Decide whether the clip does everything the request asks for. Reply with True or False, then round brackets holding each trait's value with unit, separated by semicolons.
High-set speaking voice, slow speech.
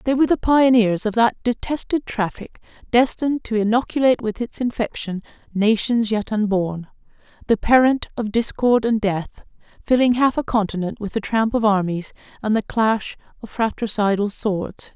False (225 Hz; 150 wpm)